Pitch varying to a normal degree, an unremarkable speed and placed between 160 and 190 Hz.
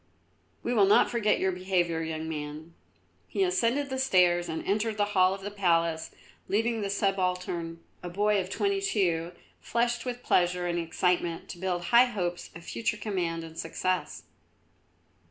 Yes: average, 3.8 semitones; average, 160 wpm; medium, 185 Hz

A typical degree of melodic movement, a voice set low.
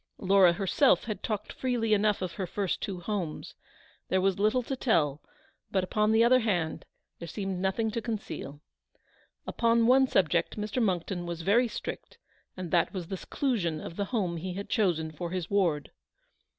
No: average, 4.2 semitones; high, 195 Hz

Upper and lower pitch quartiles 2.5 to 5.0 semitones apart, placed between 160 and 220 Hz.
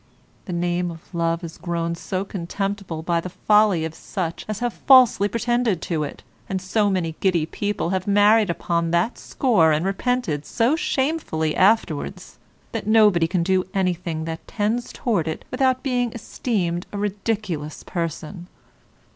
Yes: average, 4.4 semitones; medium, 185 Hz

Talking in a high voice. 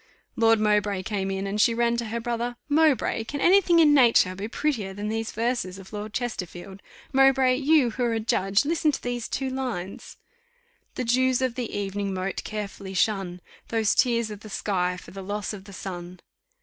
Yes: high, 220 Hz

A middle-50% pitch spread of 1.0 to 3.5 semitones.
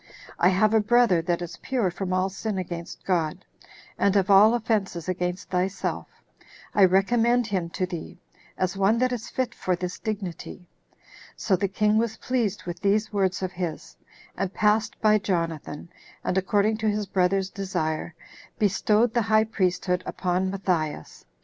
Yes: average, 3.0 semitones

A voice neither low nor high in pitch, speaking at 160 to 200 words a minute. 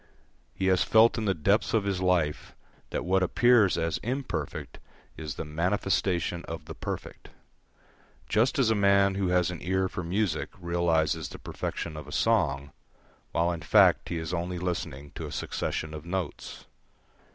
No: very low, 90 Hz; average, 165 wpm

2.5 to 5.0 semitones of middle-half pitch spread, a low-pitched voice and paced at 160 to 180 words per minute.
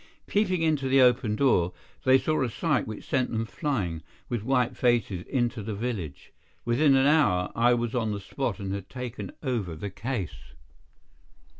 Yes: average, 4.7 semitones; low, 120 Hz; average, 170 wpm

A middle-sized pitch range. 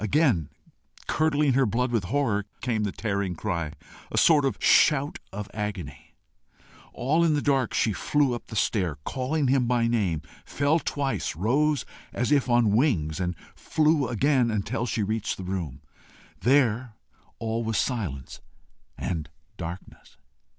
No: wide, 5.8 semitones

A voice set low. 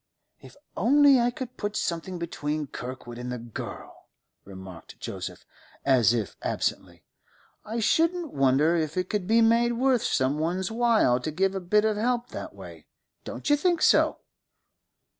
No: medium, 185 Hz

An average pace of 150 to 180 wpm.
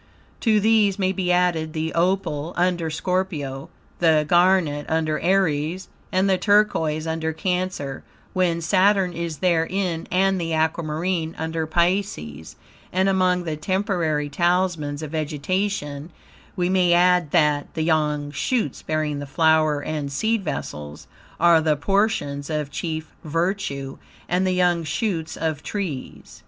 No: slow, 135 wpm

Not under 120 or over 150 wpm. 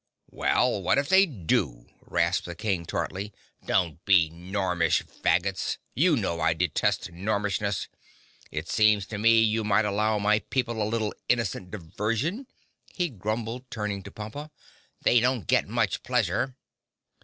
Yes: average, 145 wpm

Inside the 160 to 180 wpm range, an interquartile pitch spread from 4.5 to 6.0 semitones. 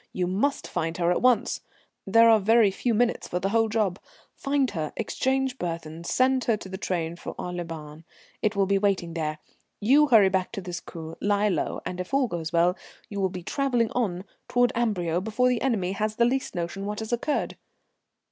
No: fast, 205 wpm; average, 5.0 semitones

